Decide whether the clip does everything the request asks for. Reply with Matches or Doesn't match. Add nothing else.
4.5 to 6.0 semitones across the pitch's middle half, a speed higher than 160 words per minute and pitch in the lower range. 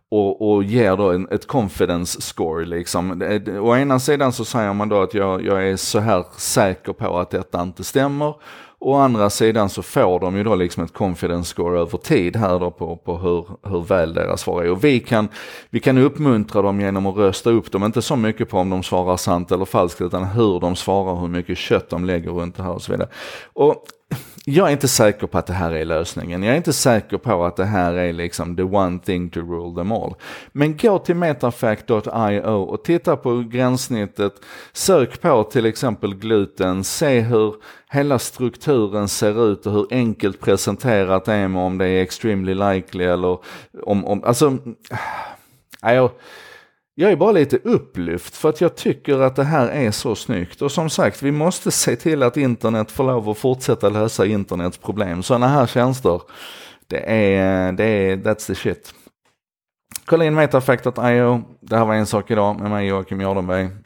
Matches